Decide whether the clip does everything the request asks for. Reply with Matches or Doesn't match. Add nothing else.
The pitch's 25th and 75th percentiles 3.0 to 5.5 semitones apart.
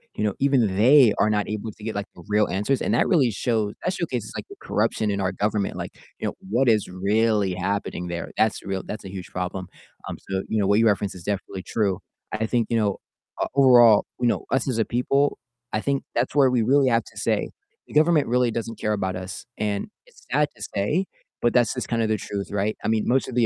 Matches